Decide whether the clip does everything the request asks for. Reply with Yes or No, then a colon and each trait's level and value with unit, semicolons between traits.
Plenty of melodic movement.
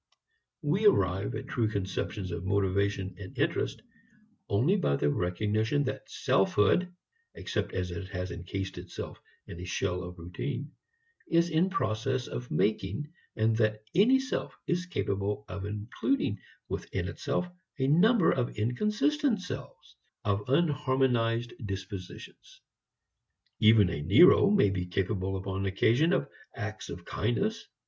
Yes: wide, 7.4 semitones